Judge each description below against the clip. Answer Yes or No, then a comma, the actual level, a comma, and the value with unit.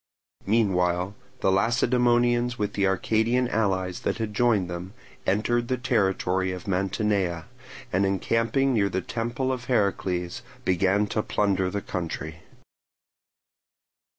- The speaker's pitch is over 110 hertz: No, low, 100 Hz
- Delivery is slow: Yes, slow, 120 wpm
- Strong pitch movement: No, average, 4.1 semitones